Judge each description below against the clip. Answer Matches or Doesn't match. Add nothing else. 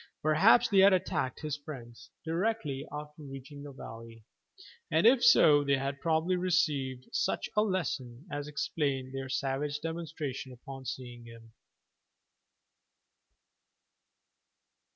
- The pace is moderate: Doesn't match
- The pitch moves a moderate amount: Matches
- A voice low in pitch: Doesn't match